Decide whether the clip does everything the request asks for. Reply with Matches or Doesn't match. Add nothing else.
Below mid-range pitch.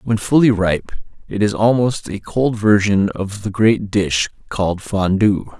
Matches